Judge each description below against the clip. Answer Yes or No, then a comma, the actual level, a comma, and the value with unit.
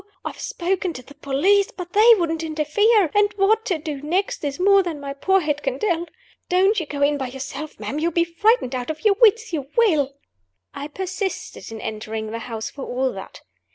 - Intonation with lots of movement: Yes, wide, 5.8 semitones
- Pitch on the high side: Yes, very high, 330 Hz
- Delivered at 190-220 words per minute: Yes, fast, 205 wpm